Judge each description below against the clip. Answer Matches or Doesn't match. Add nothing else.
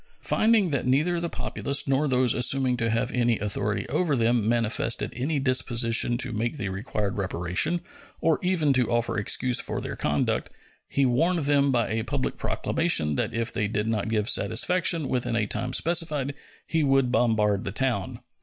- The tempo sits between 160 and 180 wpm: Matches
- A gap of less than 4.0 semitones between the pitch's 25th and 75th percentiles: Doesn't match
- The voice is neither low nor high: Doesn't match